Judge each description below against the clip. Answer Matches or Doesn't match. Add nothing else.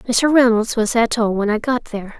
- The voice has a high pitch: Matches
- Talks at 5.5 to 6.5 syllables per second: Doesn't match